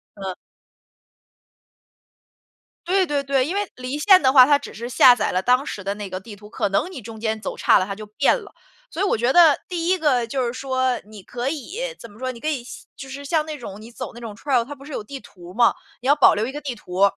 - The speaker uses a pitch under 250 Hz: No, very high, 255 Hz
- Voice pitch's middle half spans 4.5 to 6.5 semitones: Yes, average, 5.1 semitones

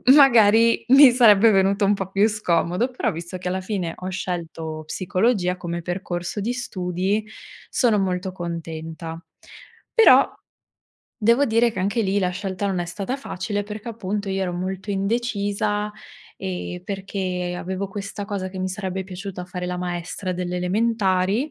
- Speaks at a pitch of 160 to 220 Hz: Yes, high, 190 Hz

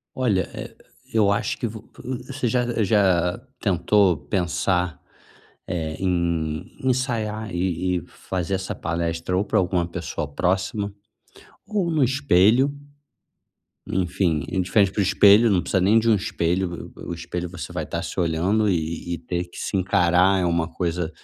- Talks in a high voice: No, very low, 95 Hz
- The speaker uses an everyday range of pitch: Yes, average, 3.4 semitones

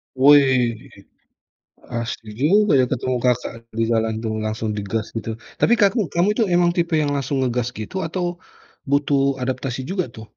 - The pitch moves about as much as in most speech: No, wide, 6.4 semitones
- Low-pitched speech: Yes, low, 130 Hz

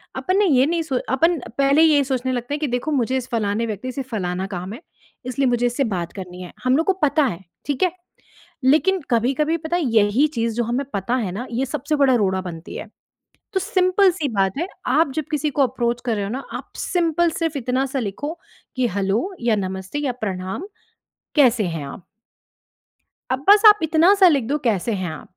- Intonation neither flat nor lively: No, wide, 6.0 semitones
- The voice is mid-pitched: No, very high, 255 Hz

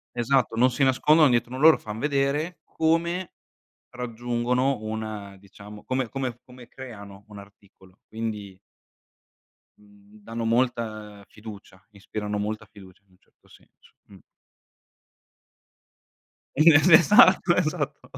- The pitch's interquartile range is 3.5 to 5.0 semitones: Yes, average, 4.2 semitones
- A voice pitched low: Yes, low, 115 Hz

